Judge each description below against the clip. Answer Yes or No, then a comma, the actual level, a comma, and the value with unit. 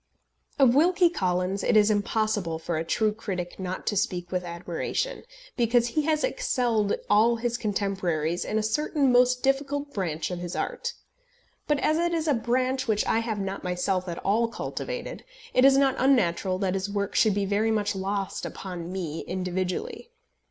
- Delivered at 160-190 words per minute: Yes, average, 175 wpm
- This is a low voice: No, high, 210 Hz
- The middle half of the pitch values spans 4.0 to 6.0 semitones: Yes, wide, 5.6 semitones